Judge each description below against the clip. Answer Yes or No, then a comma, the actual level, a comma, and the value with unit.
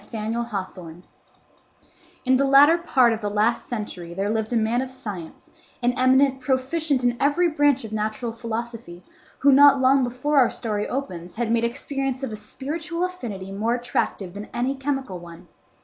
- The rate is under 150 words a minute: No, average, 170 wpm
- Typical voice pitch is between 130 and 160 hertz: No, high, 240 Hz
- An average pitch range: Yes, average, 4.1 semitones